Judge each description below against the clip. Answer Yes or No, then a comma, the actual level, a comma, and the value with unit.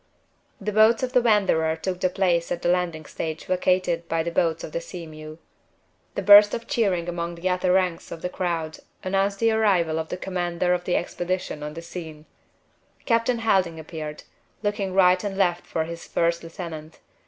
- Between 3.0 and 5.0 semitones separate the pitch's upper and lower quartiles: No, narrow, 2.6 semitones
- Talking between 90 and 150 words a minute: No, average, 190 wpm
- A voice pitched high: No, medium, 175 Hz